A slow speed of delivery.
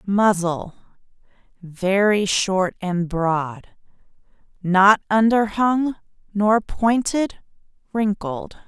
Yes: slow, 60 wpm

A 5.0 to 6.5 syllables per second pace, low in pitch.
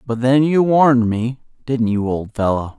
No: 4.5 syllables/s; low, 120 Hz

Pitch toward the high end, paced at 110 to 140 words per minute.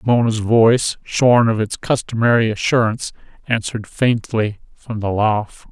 No: low, 115 Hz; slow, 135 wpm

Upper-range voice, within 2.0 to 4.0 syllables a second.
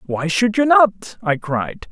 Yes: high, 195 Hz; 3.5 syllables/s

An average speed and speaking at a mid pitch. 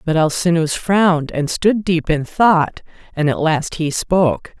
Yes: average, 170 wpm; medium, 165 Hz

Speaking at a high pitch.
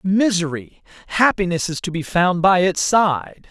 No: medium, 180 Hz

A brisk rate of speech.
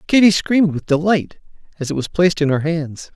Yes: fast, 210 wpm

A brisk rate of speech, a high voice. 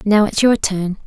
Yes: fast, 225 wpm; high, 205 Hz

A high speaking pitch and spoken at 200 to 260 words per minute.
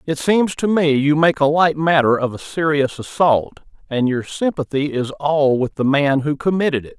No: medium, 145 Hz; fast, 205 wpm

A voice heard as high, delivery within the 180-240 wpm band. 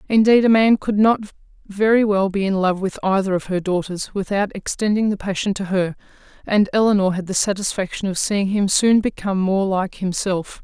Yes: high, 200 Hz; average, 190 wpm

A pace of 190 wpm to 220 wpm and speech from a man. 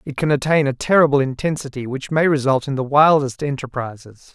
No: average, 180 wpm; male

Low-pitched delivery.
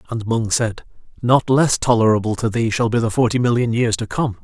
Yes: low, 115 Hz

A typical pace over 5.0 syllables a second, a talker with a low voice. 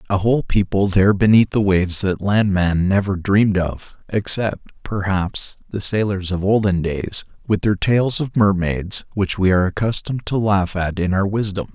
No: 4.8 syllables/s; low, 100 Hz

